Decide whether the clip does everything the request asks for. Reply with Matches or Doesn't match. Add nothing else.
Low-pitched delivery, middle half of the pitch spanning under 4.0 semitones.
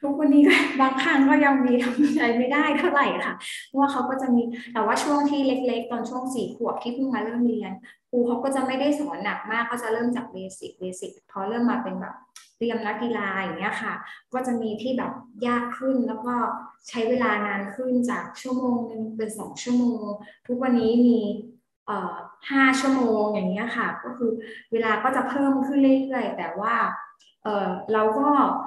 Doesn't match